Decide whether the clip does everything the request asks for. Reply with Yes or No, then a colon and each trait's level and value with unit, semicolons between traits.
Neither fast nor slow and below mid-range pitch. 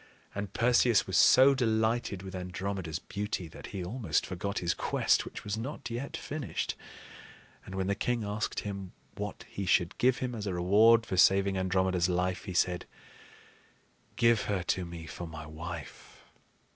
Yes: average, 165 wpm; low, 100 Hz